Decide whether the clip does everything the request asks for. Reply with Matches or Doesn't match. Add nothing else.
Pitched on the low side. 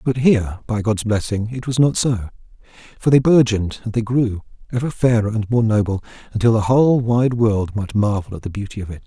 Matches